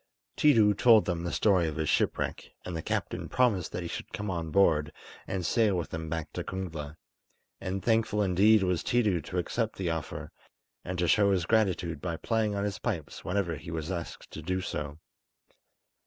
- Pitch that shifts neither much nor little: Yes, average, 3.8 semitones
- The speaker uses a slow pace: No, average, 190 wpm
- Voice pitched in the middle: No, very low, 90 Hz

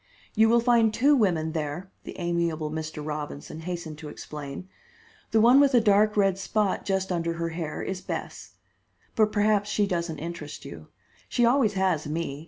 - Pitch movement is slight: No, average, 5.1 semitones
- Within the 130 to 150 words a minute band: No, average, 175 wpm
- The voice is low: No, medium, 180 Hz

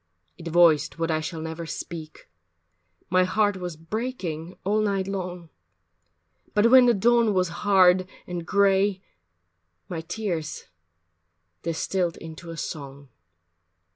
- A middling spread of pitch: Yes, average, 3.5 semitones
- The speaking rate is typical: No, slow, 120 wpm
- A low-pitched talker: No, medium, 180 Hz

